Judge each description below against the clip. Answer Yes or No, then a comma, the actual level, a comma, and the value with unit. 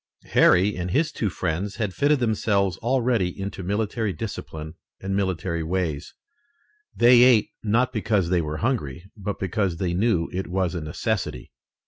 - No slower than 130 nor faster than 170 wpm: Yes, average, 150 wpm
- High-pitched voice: No, very low, 95 Hz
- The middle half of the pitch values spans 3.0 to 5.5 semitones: Yes, average, 4.2 semitones